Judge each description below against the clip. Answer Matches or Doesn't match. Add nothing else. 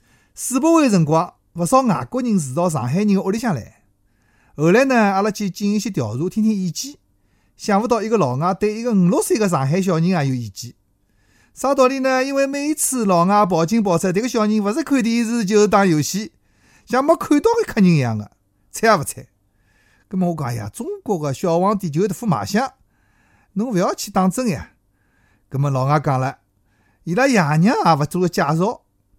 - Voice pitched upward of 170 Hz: Matches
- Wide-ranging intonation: Matches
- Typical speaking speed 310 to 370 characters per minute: Doesn't match